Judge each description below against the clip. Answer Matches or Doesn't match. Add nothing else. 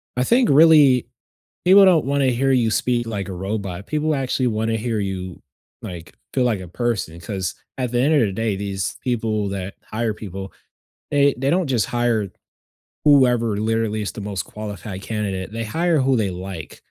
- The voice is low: Matches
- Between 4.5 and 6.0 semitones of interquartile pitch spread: Matches